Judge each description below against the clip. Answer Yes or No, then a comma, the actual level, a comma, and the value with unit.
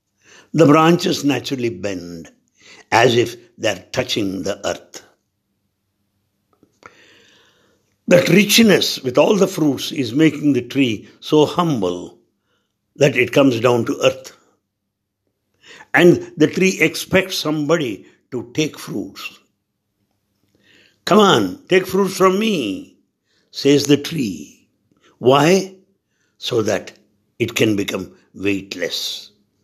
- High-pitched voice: No, medium, 140 Hz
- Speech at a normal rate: No, slow, 105 wpm